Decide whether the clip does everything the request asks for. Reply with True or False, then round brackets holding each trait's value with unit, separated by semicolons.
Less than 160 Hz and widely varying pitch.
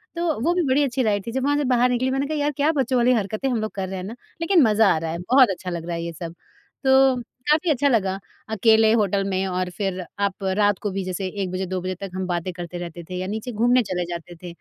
False (210 Hz; 5.8 semitones)